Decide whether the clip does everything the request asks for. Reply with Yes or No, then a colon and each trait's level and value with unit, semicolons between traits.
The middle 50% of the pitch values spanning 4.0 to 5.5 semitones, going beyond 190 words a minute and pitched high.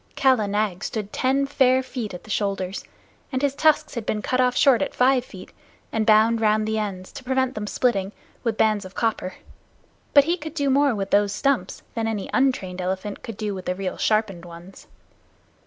Yes: average, 4.7 semitones; average, 200 wpm; high, 220 Hz